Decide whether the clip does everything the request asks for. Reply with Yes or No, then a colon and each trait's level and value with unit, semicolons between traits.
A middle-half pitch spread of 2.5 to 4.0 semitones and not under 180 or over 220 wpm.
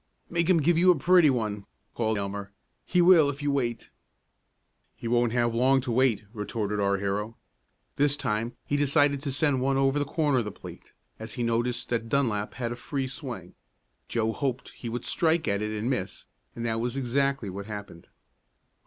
No: average, 4.4 semitones; average, 190 wpm